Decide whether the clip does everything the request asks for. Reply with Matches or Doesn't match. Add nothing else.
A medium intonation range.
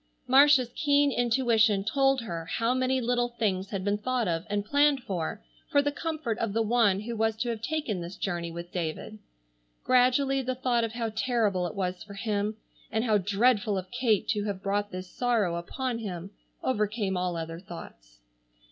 Matches